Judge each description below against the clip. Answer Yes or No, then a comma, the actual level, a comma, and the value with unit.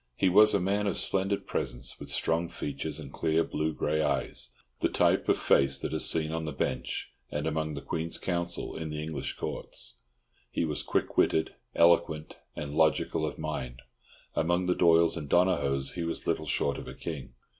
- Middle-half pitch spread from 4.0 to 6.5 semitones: No, narrow, 2.6 semitones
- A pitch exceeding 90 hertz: No, very low, 80 Hz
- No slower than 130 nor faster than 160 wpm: No, average, 185 wpm